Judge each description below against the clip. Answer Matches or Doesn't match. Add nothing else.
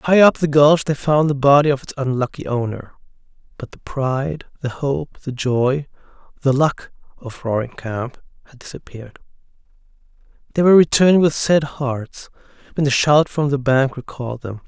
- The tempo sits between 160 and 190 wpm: Matches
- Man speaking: Matches